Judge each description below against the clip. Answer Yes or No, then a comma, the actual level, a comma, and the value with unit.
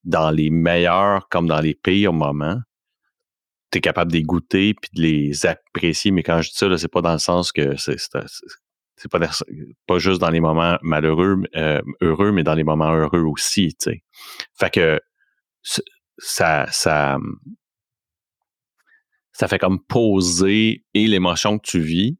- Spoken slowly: No, average, 170 wpm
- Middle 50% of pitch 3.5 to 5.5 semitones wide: Yes, average, 4.1 semitones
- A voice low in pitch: Yes, very low, 85 Hz